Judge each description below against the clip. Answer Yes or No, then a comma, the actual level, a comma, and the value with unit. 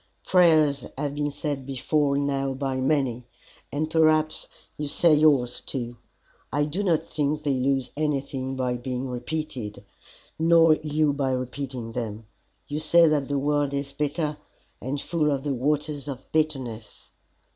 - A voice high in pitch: No, medium, 140 Hz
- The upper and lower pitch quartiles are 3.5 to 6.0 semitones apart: No, narrow, 2.6 semitones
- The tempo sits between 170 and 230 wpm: No, average, 145 wpm